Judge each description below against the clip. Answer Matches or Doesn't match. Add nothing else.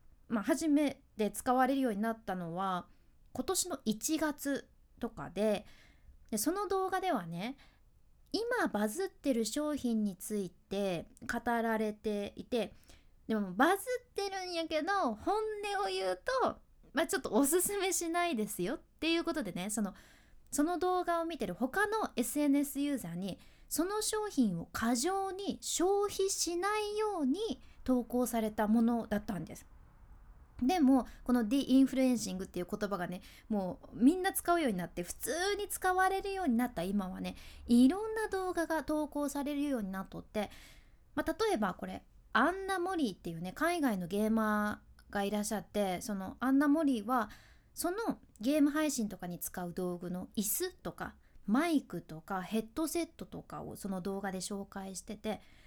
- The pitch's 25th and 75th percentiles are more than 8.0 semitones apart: Matches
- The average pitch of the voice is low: Doesn't match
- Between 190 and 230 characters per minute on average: Doesn't match